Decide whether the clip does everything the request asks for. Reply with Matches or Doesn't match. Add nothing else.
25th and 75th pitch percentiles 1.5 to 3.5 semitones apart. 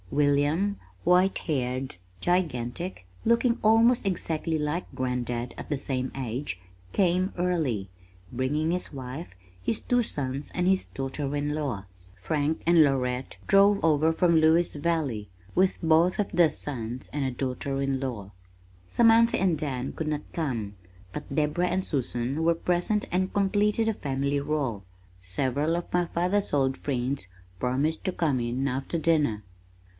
Doesn't match